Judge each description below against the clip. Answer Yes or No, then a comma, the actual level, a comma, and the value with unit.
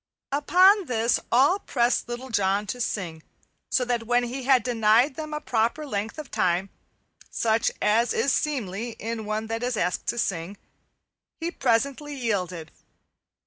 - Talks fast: No, average, 150 wpm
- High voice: Yes, high, 235 Hz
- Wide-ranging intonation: No, average, 4.0 semitones